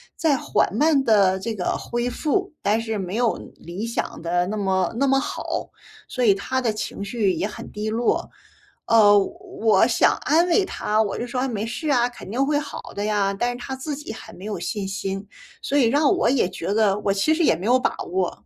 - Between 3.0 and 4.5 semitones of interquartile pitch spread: No, average, 4.9 semitones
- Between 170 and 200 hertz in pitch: No, high, 225 Hz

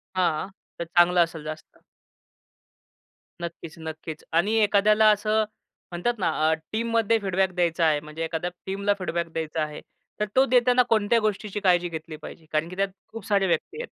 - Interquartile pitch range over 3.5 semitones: Yes, average, 4.6 semitones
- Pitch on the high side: No, medium, 180 Hz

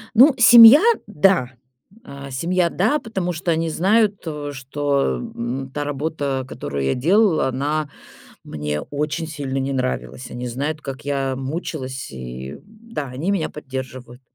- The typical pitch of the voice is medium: Yes, medium, 145 Hz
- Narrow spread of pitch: No, average, 4.9 semitones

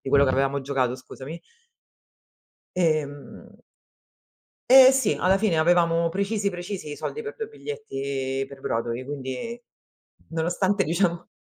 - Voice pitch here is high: No, medium, 165 Hz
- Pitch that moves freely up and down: Yes, wide, 6.4 semitones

